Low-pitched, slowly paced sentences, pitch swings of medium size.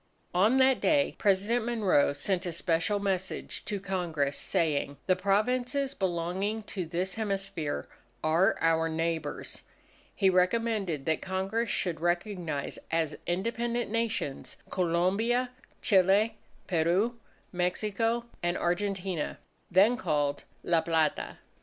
No: high, 190 Hz; slow, 110 wpm; average, 4.4 semitones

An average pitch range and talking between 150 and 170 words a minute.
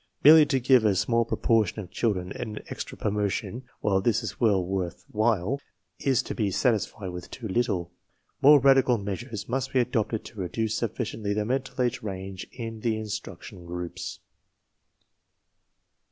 Yes: average, 3.8 semitones; average, 155 wpm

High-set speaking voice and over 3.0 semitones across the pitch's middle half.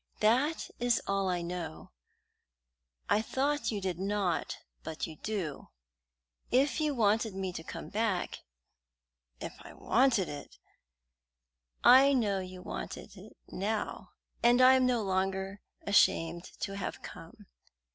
Yes: high, 200 Hz; average, 4.9 semitones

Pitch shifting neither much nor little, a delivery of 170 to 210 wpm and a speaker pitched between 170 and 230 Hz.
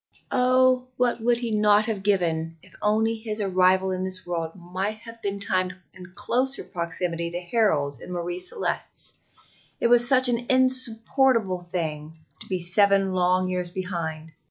No: average, 4.4 semitones; average, 155 wpm; high, 190 Hz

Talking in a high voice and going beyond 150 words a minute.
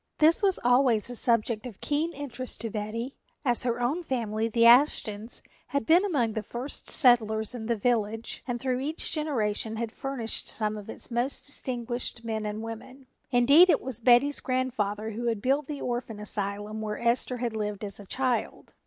Yes: high, 240 Hz; average, 180 wpm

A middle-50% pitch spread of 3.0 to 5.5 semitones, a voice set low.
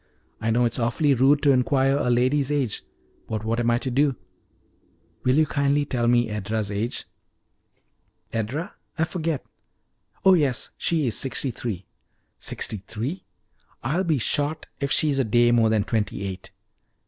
Yes: average, 4.2 semitones; low, 125 Hz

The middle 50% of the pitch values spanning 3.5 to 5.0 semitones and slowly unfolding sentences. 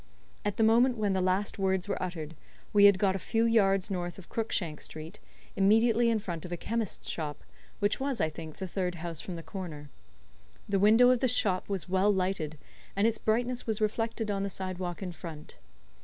No: average, 3.8 semitones; average, 200 wpm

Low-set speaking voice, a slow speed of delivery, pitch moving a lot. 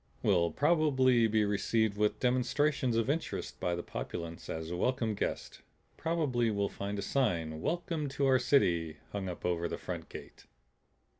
No: low, 110 Hz; average, 155 wpm; wide, 7.1 semitones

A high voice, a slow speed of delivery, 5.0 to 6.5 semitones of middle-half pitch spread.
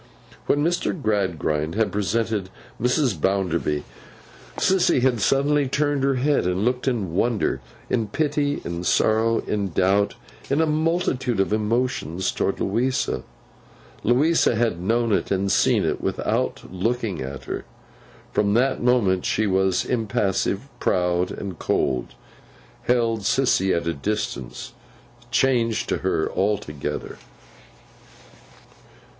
No: low, 110 Hz; slow, 115 wpm; average, 5.3 semitones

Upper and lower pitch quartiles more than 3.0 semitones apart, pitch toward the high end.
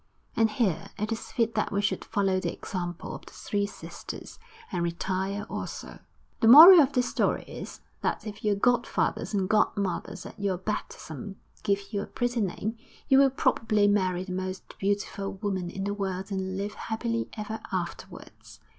No: narrow, 2.6 semitones; high, 205 Hz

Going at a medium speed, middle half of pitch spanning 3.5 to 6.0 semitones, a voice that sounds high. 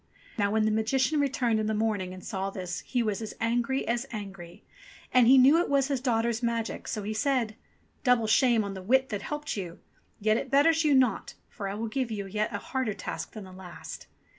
No: fast, 220 wpm; average, 4.1 semitones; high, 225 Hz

